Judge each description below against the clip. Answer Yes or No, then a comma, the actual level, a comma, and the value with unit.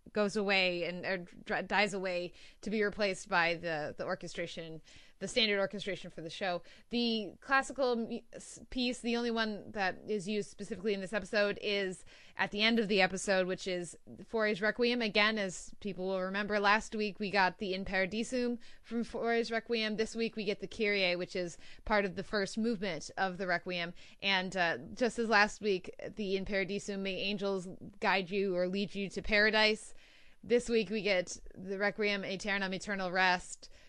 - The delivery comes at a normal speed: Yes, average, 180 wpm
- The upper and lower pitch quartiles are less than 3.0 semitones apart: Yes, narrow, 2.6 semitones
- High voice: Yes, high, 200 Hz